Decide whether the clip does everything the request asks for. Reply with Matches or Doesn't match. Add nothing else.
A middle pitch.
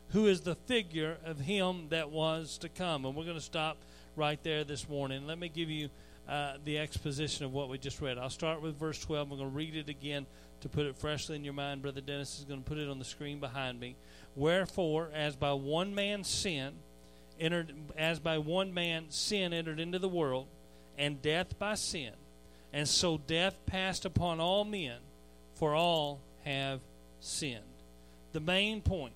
Matches